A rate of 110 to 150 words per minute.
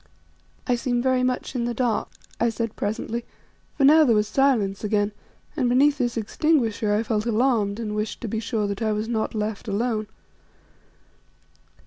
No: average, 170 wpm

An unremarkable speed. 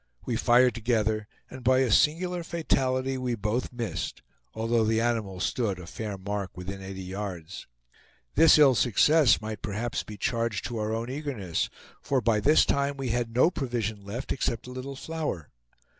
Yes: average, 170 wpm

